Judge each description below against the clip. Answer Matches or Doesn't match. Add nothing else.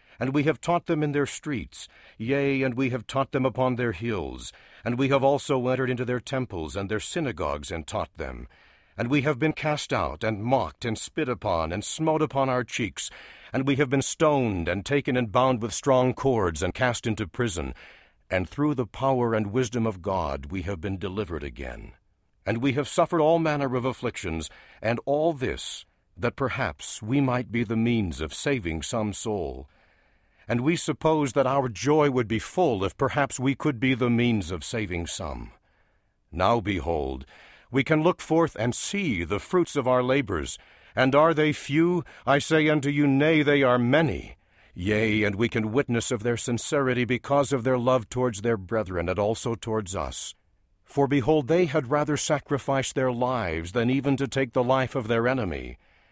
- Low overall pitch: Matches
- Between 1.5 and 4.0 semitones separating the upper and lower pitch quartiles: Doesn't match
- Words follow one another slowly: Doesn't match